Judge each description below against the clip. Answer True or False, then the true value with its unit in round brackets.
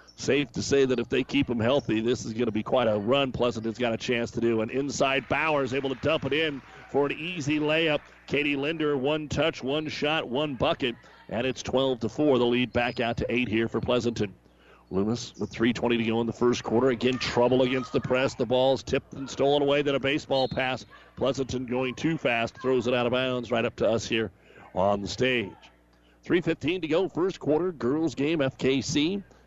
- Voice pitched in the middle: False (130 Hz)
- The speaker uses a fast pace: True (215 wpm)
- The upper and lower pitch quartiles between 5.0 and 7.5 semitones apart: False (2.9 semitones)